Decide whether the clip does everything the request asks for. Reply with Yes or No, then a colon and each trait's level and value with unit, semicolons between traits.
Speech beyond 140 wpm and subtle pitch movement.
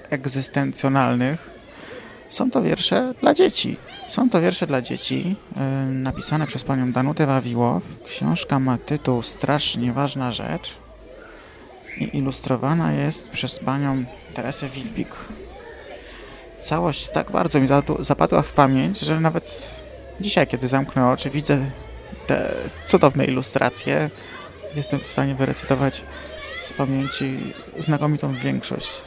No: slow, 110 wpm; narrow, 2.1 semitones